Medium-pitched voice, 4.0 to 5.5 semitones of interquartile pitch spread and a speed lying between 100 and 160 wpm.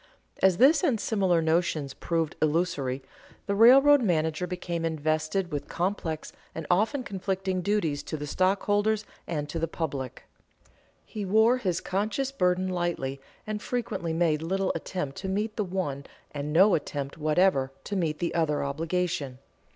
Yes: medium, 175 Hz; average, 4.4 semitones; average, 150 wpm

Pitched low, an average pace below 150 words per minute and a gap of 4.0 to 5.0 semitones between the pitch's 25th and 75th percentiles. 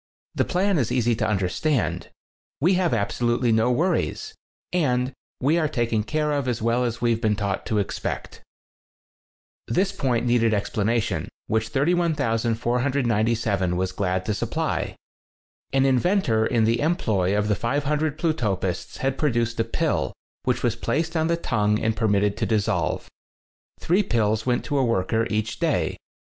No: low, 120 Hz; average, 155 wpm; average, 4.6 semitones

